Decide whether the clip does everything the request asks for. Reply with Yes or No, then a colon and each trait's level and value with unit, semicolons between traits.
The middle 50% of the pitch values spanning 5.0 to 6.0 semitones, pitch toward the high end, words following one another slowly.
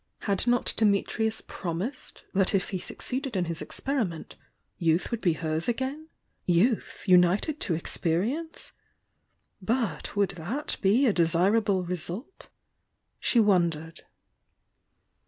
Yes: wide, 5.6 semitones; high, 195 Hz; slow, 120 wpm